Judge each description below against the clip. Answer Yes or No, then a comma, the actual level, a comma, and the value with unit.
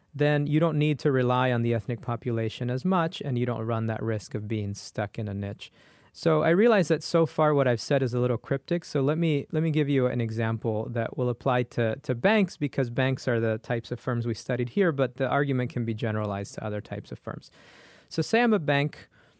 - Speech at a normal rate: No, fast, 240 wpm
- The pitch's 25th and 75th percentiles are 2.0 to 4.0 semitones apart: No, average, 4.5 semitones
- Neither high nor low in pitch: No, low, 125 Hz